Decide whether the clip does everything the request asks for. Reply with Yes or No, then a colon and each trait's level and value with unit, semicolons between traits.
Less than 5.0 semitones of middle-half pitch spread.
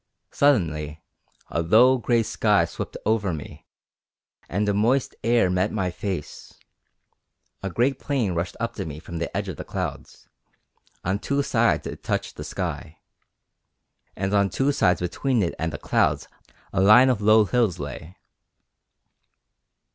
No: wide, 5.5 semitones